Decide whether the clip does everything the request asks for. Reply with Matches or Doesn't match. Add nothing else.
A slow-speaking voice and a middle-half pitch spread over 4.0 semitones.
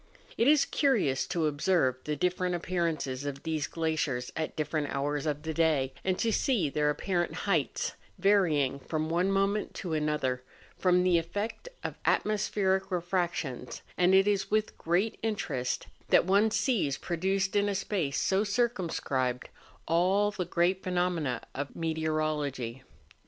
Doesn't match